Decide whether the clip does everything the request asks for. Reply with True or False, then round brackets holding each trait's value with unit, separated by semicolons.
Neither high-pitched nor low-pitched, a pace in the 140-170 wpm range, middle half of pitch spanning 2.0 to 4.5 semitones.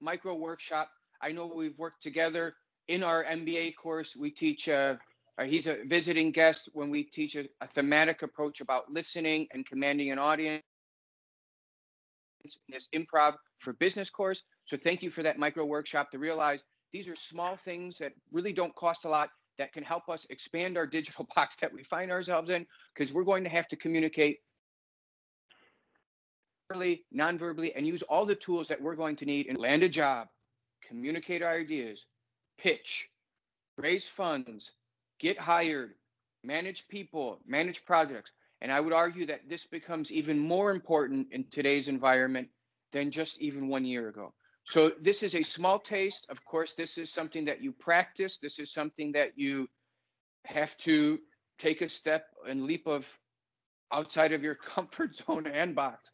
True (160 Hz; 165 wpm; 2.9 semitones)